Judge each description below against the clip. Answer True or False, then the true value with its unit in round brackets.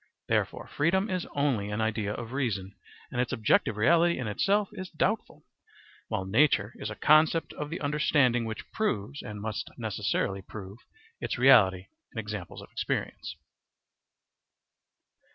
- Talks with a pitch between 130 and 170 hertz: False (120 Hz)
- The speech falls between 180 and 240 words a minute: False (140 wpm)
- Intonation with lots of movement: True (6.7 semitones)